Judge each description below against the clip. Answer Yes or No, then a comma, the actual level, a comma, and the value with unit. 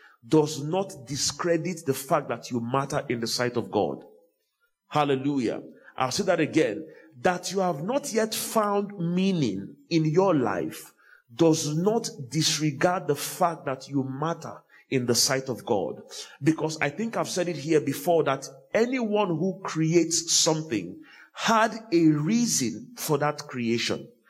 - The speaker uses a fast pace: No, average, 150 wpm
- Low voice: No, medium, 160 Hz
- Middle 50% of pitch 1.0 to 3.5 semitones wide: No, average, 5.1 semitones